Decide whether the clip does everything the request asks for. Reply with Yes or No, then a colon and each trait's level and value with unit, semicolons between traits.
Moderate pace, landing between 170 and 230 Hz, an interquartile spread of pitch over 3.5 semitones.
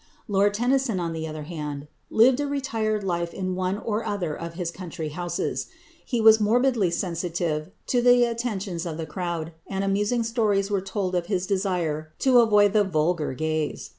Yes: average, 175 wpm; high, 190 Hz; average, 4.5 semitones